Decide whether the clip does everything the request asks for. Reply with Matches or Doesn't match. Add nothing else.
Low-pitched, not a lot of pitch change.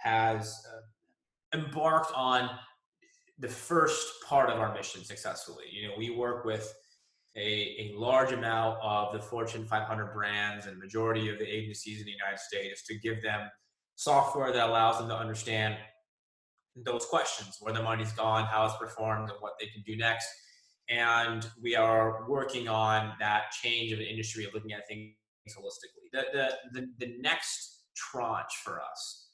Matches